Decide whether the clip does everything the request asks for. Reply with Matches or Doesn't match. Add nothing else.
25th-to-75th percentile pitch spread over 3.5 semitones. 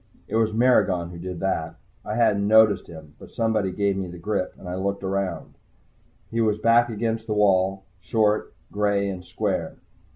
Doesn't match